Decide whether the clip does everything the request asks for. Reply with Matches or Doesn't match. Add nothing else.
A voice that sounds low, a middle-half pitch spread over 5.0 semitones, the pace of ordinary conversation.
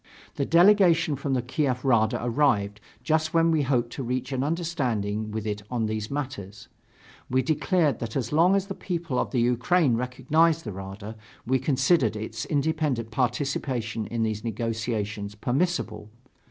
Matches